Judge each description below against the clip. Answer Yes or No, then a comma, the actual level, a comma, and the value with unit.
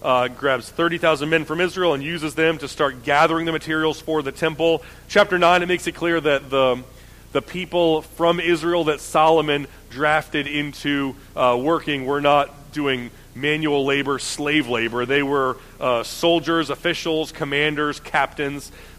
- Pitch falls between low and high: Yes, medium, 150 Hz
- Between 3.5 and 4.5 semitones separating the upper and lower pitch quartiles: No, average, 2.8 semitones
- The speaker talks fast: No, average, 160 wpm